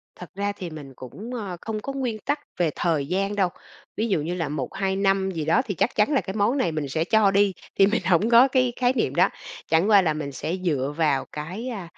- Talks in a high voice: Yes, high, 195 Hz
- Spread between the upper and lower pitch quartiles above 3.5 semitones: Yes, average, 5.2 semitones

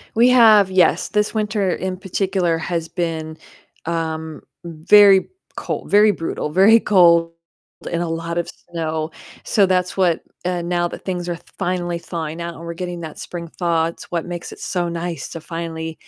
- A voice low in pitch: No, medium, 175 Hz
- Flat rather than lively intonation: Yes, narrow, 2.2 semitones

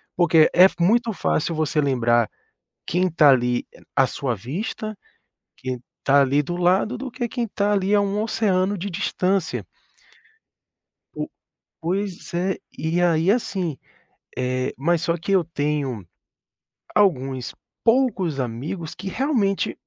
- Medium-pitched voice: Yes, medium, 175 Hz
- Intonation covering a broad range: Yes, wide, 6.0 semitones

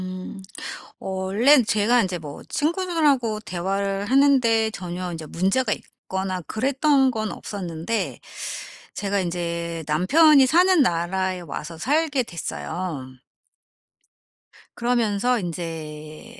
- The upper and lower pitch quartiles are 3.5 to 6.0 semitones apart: No, wide, 6.5 semitones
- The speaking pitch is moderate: No, high, 195 Hz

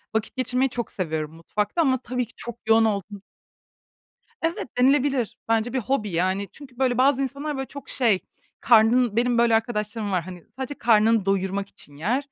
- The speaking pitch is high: Yes, high, 230 Hz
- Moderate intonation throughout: Yes, average, 4.3 semitones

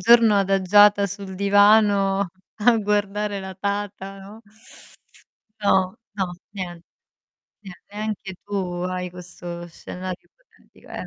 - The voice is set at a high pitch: Yes, high, 195 Hz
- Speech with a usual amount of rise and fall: No, narrow, 1.8 semitones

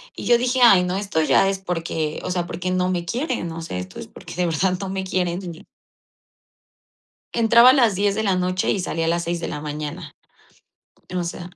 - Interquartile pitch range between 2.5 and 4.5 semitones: Yes, average, 2.8 semitones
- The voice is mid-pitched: Yes, medium, 180 Hz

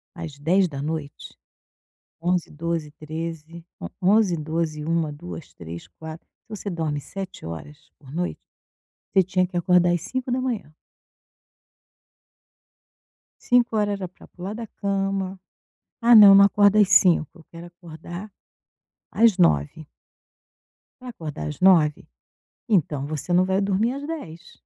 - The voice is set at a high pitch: No, medium, 175 Hz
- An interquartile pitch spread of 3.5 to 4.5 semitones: Yes, average, 4.1 semitones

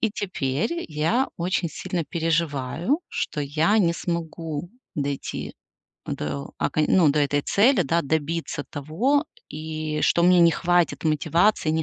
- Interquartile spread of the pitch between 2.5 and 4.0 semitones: Yes, average, 2.9 semitones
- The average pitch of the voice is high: No, medium, 165 Hz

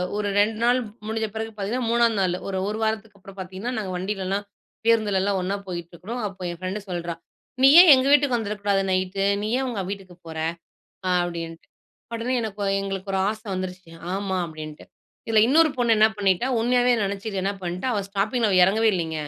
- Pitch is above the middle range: Yes, high, 200 Hz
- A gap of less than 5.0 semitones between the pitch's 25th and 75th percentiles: Yes, average, 3.2 semitones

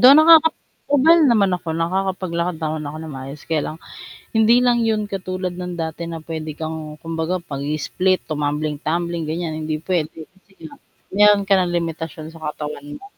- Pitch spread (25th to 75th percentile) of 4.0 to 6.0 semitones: No, average, 3.4 semitones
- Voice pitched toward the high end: No, medium, 170 Hz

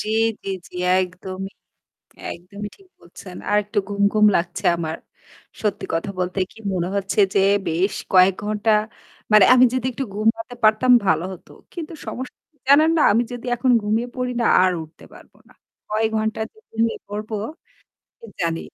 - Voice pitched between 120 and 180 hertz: No, high, 210 Hz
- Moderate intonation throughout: Yes, average, 3.6 semitones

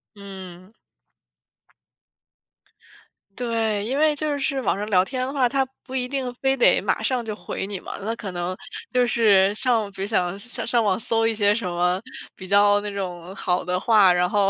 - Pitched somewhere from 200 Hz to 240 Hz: Yes, high, 210 Hz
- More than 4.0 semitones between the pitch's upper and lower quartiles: Yes, average, 4.5 semitones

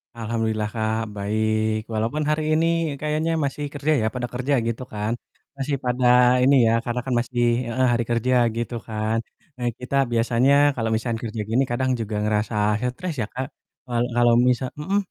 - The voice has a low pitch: Yes, low, 120 Hz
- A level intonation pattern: No, average, 3.3 semitones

